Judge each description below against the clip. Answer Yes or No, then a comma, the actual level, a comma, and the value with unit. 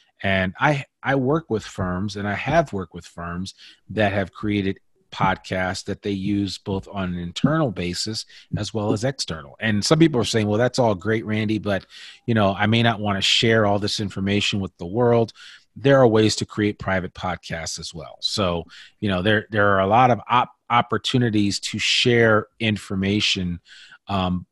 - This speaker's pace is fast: No, average, 190 wpm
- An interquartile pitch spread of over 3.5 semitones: No, average, 2.7 semitones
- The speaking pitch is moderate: No, low, 100 Hz